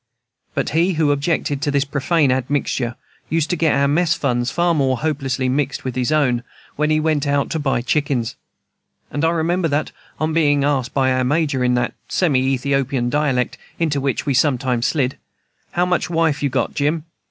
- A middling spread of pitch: Yes, average, 3.2 semitones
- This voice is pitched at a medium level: Yes, medium, 145 Hz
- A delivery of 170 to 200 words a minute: Yes, average, 185 wpm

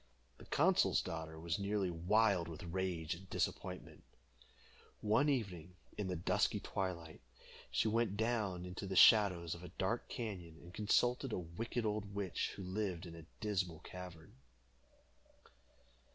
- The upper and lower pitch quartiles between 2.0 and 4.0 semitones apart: Yes, average, 3.7 semitones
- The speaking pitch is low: Yes, very low, 95 Hz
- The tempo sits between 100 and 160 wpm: Yes, average, 140 wpm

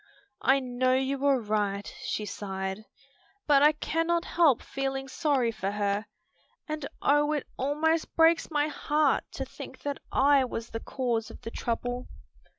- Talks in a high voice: Yes, very high, 270 Hz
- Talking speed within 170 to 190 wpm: No, average, 155 wpm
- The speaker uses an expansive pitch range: No, average, 4.6 semitones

